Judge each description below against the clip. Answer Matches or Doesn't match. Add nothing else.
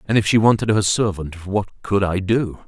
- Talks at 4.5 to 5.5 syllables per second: Matches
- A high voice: Doesn't match